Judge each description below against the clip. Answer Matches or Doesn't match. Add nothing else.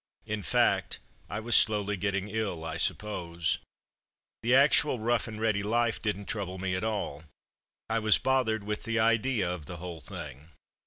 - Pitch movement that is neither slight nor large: Matches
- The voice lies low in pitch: Matches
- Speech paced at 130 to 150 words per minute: Doesn't match